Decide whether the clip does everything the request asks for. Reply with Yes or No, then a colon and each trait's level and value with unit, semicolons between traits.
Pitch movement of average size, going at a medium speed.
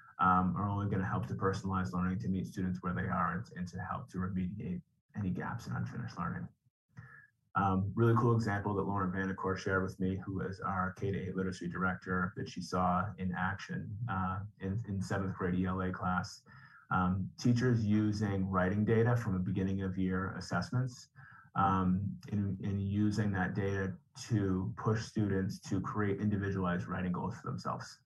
No: narrow, 2.0 semitones; average, 175 wpm